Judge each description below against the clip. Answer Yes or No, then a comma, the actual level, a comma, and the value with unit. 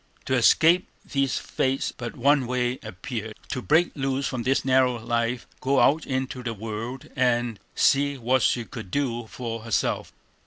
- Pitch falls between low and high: No, low, 125 Hz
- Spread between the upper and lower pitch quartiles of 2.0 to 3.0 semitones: Yes, narrow, 2.4 semitones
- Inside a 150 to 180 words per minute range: Yes, average, 160 wpm